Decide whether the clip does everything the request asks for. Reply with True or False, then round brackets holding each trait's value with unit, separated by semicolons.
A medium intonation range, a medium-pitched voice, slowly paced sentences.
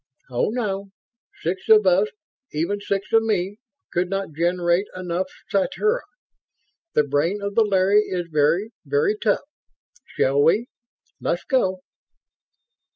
False (3.4 semitones; 195 Hz; 125 wpm)